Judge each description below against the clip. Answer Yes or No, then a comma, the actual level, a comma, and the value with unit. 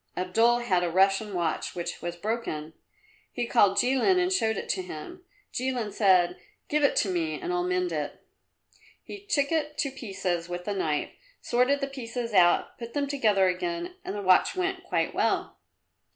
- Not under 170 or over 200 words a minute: Yes, average, 180 wpm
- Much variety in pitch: Yes, wide, 7.7 semitones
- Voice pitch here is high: Yes, high, 220 Hz